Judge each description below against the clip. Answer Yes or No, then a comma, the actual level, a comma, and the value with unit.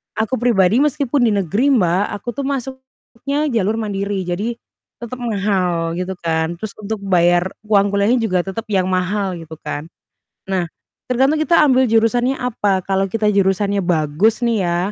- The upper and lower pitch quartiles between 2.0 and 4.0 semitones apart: No, average, 4.6 semitones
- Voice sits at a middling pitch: No, high, 205 Hz